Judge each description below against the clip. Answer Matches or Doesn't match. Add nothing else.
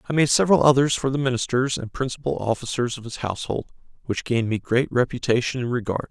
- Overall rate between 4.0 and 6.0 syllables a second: Doesn't match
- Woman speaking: Doesn't match